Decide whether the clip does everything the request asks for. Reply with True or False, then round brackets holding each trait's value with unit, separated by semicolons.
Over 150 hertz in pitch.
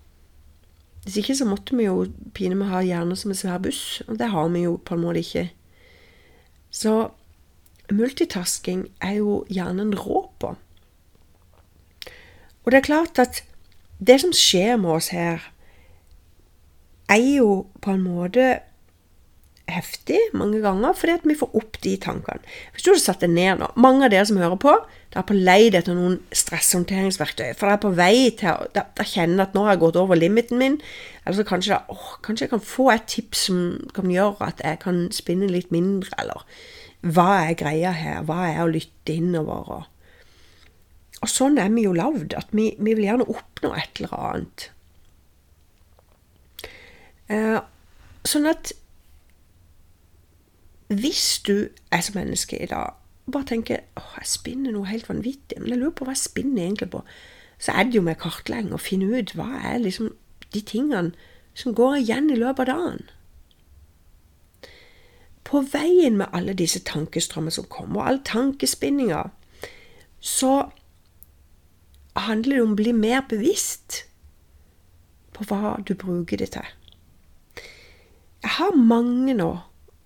True (185 Hz)